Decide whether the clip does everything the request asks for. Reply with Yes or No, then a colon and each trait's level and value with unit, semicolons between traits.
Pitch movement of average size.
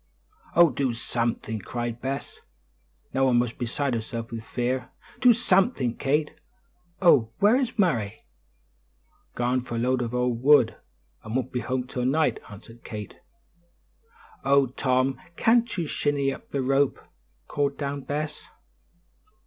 Yes: average, 3.3 semitones